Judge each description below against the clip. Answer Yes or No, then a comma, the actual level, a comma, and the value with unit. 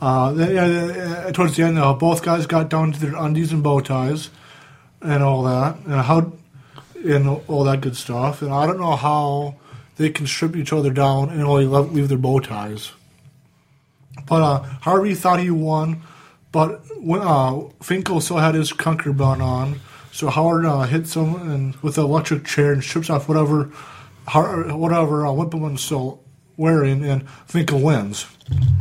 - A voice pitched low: No, medium, 150 Hz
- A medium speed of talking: Yes, average, 170 wpm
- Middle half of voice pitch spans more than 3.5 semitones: No, average, 2.9 semitones